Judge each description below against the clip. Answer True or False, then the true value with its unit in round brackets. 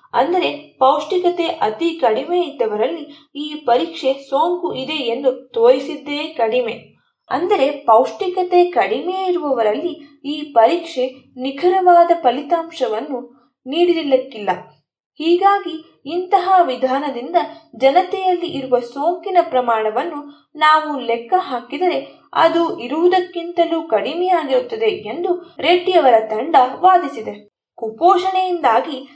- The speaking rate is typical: True (80 wpm)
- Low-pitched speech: False (310 Hz)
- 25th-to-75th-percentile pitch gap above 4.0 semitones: True (5.5 semitones)